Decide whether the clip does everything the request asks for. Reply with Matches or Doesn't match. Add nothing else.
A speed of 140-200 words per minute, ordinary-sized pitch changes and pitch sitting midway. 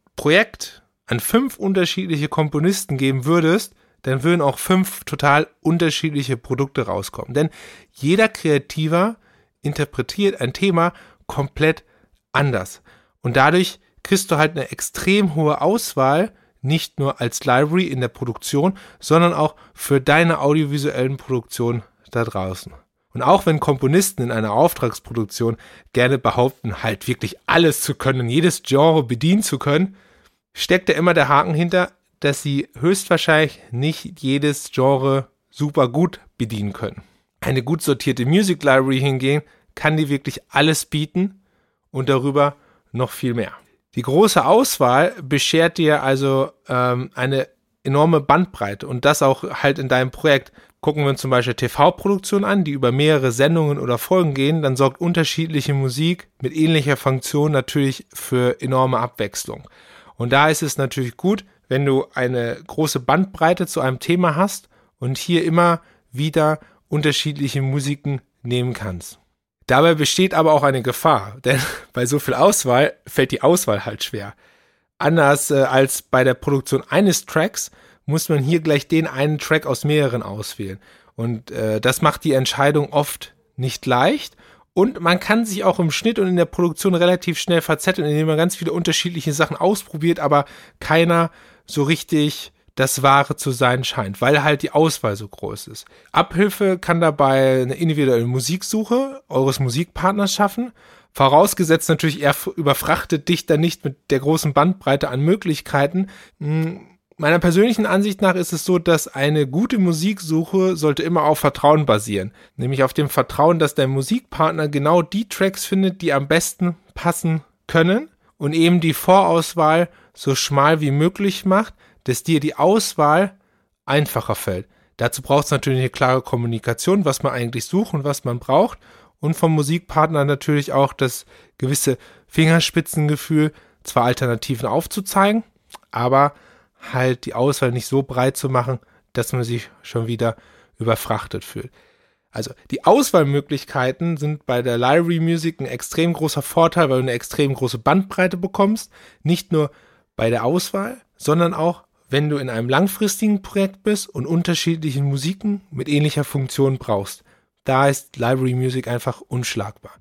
Matches